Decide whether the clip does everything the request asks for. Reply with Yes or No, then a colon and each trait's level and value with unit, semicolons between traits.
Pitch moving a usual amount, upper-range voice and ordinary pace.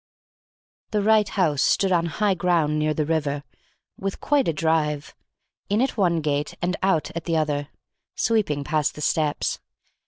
No: average, 4.4 semitones; medium, 160 Hz; average, 160 wpm